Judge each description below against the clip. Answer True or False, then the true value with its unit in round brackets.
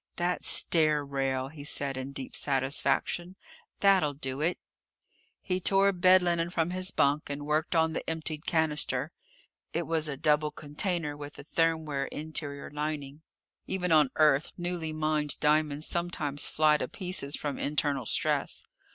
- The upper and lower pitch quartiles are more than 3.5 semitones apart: False (2.8 semitones)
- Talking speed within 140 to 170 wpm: True (150 wpm)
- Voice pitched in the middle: True (155 Hz)